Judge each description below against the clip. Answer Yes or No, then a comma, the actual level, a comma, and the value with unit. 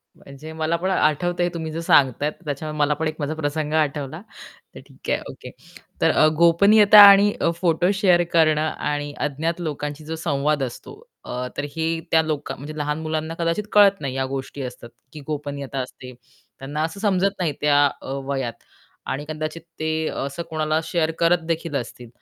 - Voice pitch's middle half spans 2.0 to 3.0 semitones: Yes, narrow, 2.5 semitones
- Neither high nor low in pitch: Yes, medium, 155 Hz